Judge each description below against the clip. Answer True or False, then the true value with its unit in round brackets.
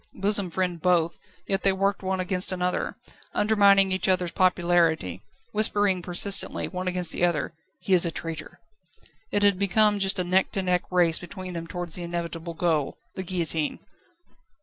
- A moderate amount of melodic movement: False (2.1 semitones)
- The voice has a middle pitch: True (180 Hz)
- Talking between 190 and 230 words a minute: False (165 wpm)